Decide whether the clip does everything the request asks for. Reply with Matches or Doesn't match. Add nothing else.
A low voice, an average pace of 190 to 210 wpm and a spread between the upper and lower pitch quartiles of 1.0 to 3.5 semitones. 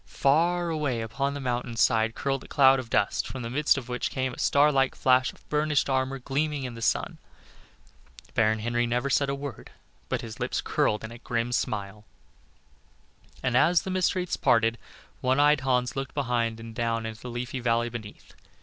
Matches